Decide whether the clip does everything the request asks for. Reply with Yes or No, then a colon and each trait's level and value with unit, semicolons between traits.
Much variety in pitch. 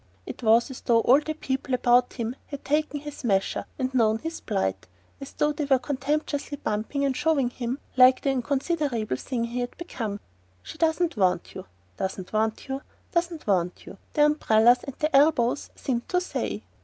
No: average, 4.4 semitones